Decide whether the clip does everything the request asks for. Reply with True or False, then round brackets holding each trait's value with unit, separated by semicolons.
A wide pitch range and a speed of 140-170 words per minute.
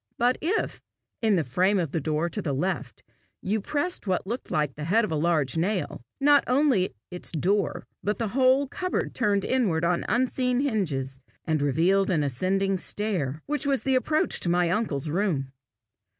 False (7.1 semitones; 180 wpm)